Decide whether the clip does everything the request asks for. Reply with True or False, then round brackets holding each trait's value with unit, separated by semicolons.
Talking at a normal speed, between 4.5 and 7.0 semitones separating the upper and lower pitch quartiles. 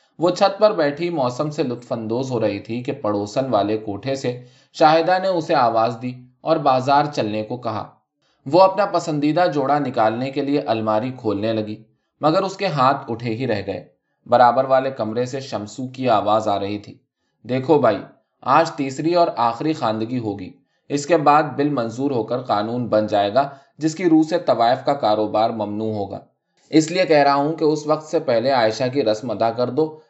False (195 wpm; 5.4 semitones)